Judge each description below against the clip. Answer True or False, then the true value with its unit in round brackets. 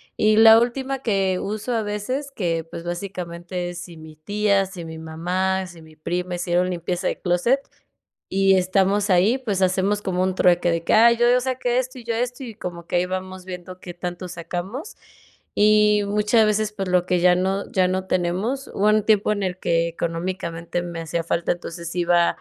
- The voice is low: False (185 Hz)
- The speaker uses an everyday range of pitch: True (3.3 semitones)